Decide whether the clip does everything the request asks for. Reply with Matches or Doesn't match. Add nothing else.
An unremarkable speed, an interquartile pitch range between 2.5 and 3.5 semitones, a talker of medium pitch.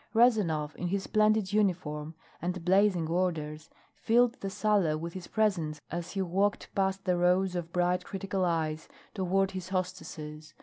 Matches